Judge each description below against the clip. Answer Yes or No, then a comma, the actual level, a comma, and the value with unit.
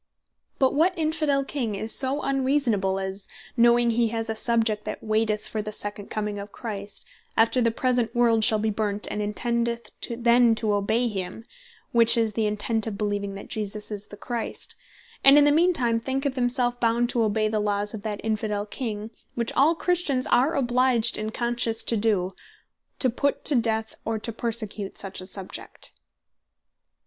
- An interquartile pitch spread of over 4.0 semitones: No, narrow, 2.6 semitones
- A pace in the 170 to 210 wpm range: Yes, average, 175 wpm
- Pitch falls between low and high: No, high, 225 Hz